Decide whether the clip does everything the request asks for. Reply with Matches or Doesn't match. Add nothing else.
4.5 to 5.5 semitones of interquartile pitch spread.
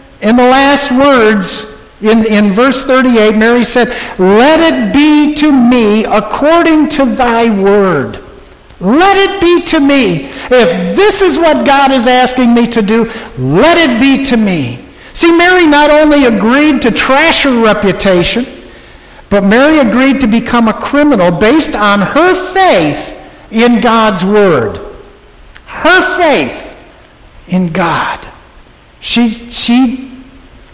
Matches